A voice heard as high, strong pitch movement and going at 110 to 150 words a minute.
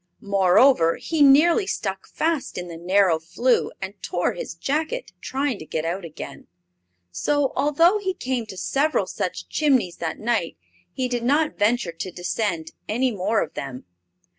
No: high, 225 Hz; wide, 8.3 semitones; average, 160 wpm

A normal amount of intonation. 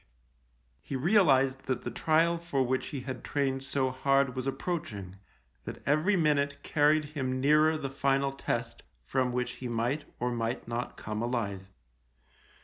Yes: average, 3.0 semitones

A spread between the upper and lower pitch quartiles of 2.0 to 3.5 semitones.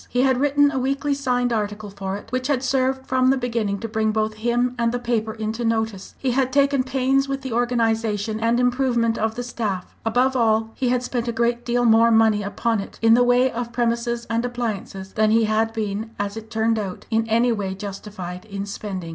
Yes: narrow, 2.4 semitones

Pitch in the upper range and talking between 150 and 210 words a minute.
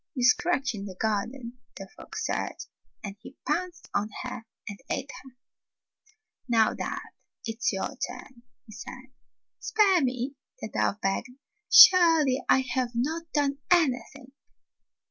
No: very high, 255 Hz; slow, 135 wpm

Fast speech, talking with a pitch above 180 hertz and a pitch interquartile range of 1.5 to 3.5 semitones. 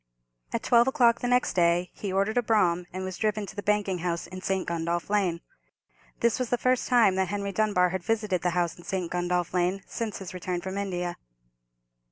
Yes: fast, 210 wpm; high, 190 Hz; average, 3.2 semitones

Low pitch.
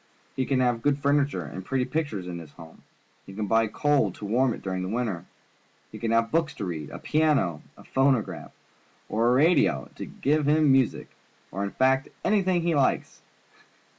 Yes: low, 125 Hz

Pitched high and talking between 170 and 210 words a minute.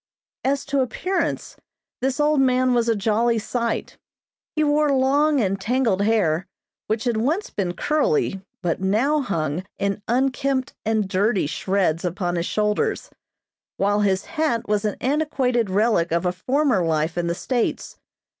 No: high, 225 Hz; average, 150 wpm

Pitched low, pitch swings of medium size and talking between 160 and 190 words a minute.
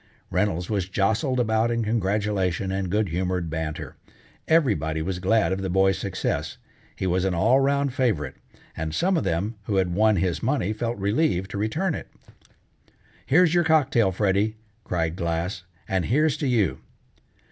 Yes: low, 100 Hz; average, 4.6 semitones; average, 165 wpm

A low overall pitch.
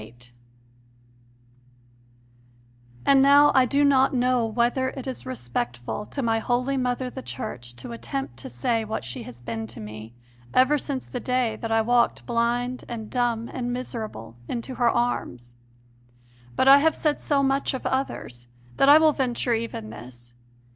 No: high, 240 Hz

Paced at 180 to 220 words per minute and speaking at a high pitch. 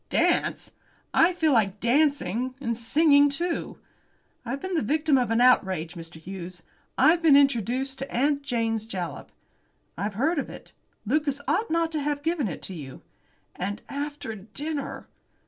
No: average, 150 wpm; very high, 265 Hz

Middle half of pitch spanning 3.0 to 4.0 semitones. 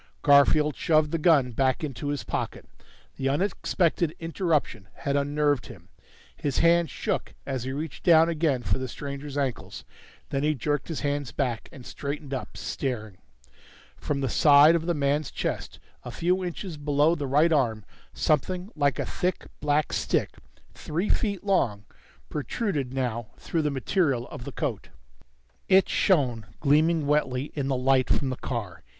Yes: average, 3.5 semitones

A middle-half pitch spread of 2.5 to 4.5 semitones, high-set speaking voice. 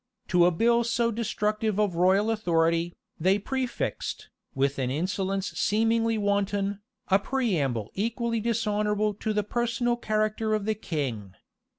Yes: average, 4.0 semitones; high, 210 Hz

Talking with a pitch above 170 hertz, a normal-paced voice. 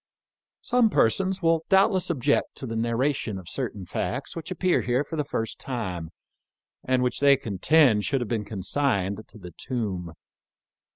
No: low, 125 Hz; average, 170 wpm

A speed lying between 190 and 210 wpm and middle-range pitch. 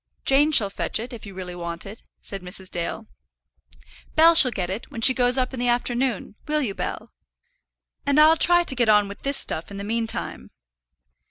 No: average, 200 wpm; high, 235 Hz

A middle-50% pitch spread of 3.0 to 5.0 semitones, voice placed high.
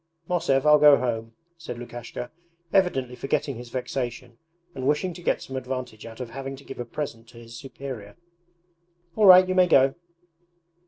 No: average, 3.7 semitones; low, 130 Hz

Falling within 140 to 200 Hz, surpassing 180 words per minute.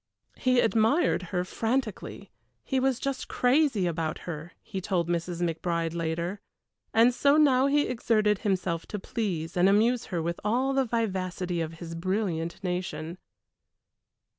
No: high, 190 Hz; average, 140 wpm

